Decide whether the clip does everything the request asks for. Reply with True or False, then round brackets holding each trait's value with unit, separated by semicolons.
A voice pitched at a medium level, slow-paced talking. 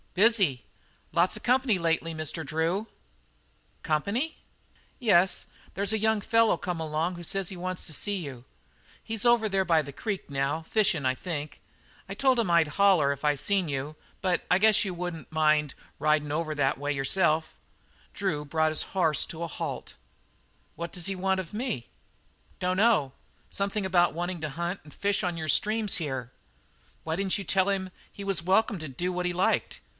False (175 Hz; 180 wpm)